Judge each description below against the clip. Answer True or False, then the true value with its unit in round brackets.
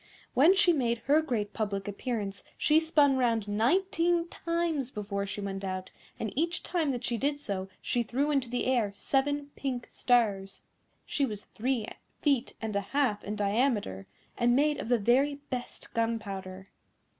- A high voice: True (240 Hz)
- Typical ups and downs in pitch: False (5.8 semitones)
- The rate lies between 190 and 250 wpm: False (165 wpm)